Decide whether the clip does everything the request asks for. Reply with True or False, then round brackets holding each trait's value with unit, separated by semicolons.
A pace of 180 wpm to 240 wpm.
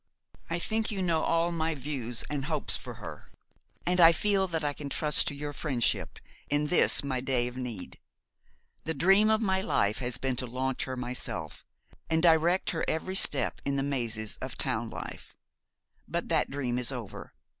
True (185 wpm)